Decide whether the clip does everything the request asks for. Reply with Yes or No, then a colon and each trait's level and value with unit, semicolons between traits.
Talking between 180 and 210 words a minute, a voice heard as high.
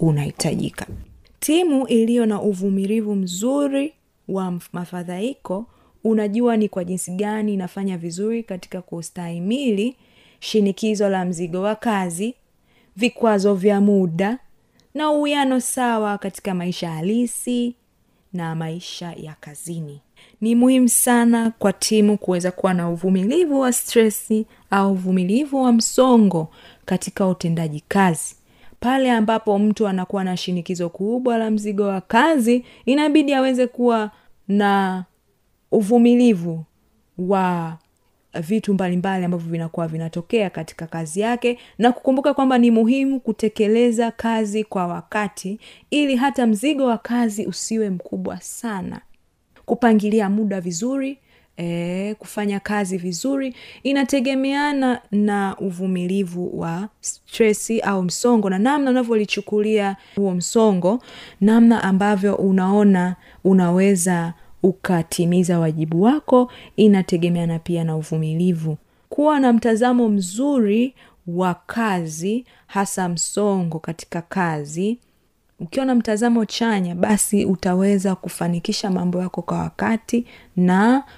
No: average, 110 wpm; high, 205 Hz